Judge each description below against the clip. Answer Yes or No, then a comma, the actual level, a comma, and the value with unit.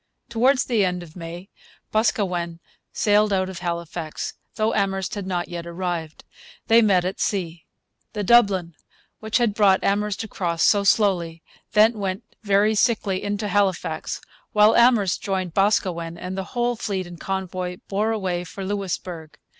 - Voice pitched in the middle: No, high, 195 Hz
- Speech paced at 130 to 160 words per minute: Yes, average, 150 wpm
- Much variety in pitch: No, average, 3.1 semitones